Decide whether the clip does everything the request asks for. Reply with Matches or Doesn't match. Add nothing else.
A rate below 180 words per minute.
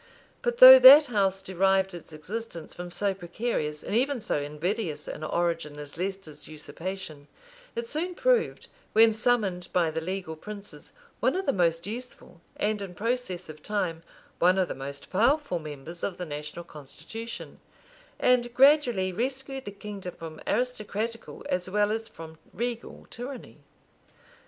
Matches